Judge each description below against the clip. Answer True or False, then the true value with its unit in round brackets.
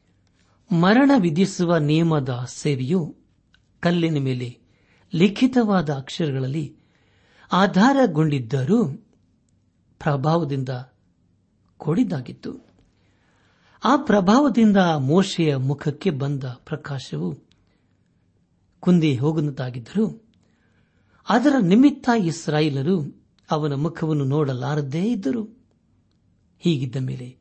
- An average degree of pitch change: False (6.4 semitones)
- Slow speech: True (60 wpm)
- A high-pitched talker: False (155 Hz)